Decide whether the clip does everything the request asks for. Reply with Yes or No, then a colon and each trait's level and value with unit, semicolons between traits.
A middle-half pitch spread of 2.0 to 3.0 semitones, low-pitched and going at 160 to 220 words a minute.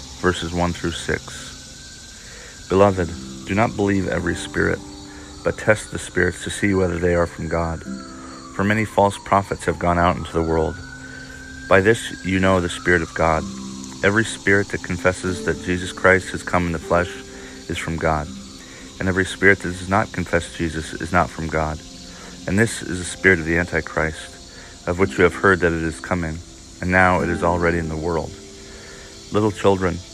Yes: narrow, 2.6 semitones; very low, 85 Hz; average, 185 wpm